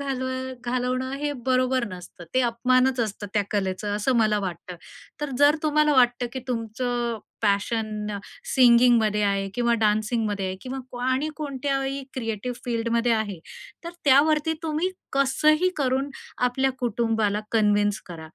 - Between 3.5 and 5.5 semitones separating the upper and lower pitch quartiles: Yes, average, 3.8 semitones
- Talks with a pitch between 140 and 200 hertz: No, high, 245 Hz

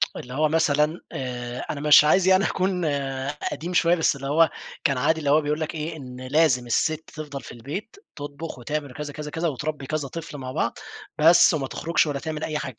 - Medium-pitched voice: Yes, medium, 150 Hz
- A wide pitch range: No, average, 2.7 semitones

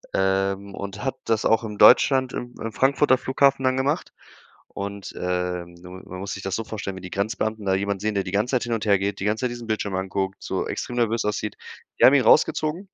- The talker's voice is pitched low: Yes, low, 105 Hz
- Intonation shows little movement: No, average, 3.9 semitones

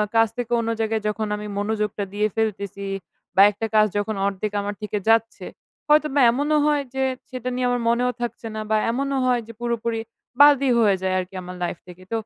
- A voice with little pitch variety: No, average, 3.2 semitones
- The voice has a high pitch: Yes, high, 225 Hz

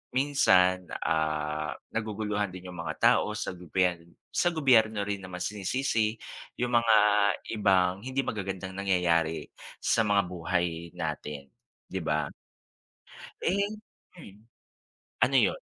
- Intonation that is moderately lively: Yes, average, 3.9 semitones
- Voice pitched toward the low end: Yes, very low, 95 Hz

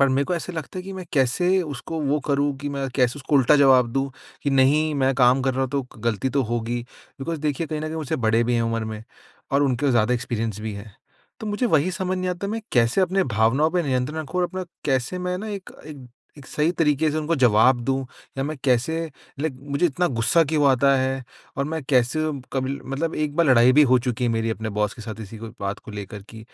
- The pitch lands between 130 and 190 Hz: Yes, low, 135 Hz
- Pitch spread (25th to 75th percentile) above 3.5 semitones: Yes, average, 4.4 semitones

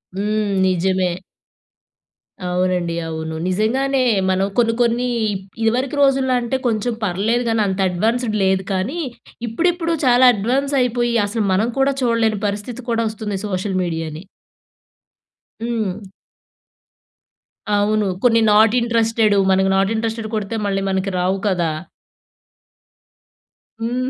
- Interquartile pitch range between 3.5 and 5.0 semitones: Yes, average, 4.0 semitones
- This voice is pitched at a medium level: No, high, 215 Hz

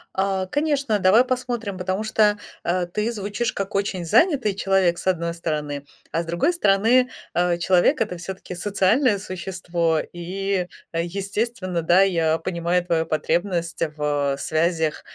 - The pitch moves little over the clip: No, average, 3.3 semitones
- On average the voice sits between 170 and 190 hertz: Yes, medium, 185 Hz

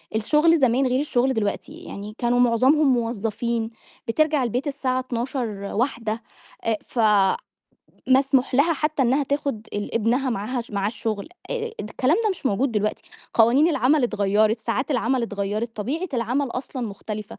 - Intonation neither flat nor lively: Yes, average, 3.7 semitones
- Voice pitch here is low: No, high, 245 Hz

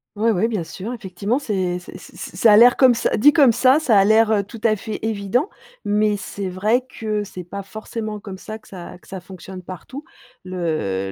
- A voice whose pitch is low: No, high, 210 Hz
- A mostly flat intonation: No, average, 3.5 semitones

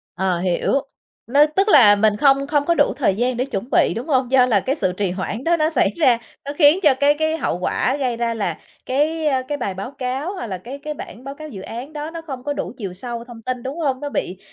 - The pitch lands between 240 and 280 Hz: Yes, very high, 260 Hz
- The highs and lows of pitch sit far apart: No, average, 4.4 semitones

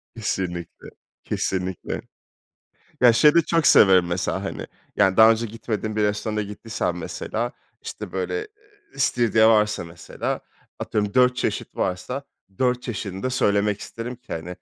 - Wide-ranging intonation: No, average, 4.0 semitones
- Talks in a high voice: No, low, 110 Hz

